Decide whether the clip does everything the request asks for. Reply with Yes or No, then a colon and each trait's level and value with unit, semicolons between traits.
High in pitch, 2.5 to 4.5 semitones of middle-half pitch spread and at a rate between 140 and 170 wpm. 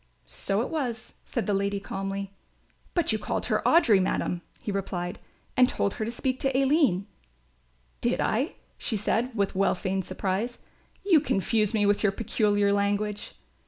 Yes: high, 205 Hz; average, 3.3 semitones; average, 165 wpm